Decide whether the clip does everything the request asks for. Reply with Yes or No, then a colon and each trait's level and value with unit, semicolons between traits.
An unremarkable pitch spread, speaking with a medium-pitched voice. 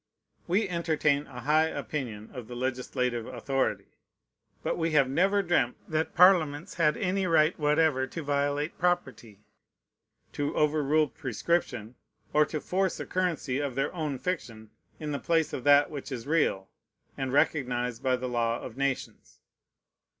Yes: average, 4.1 semitones; medium, 145 Hz